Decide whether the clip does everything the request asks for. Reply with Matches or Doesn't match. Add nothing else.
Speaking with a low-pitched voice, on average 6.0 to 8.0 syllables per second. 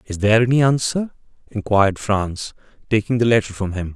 Doesn't match